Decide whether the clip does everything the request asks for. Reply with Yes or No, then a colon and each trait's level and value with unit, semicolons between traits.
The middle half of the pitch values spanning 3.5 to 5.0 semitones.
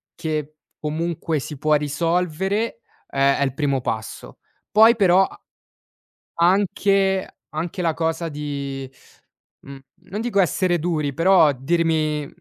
Yes: average, 3.9 semitones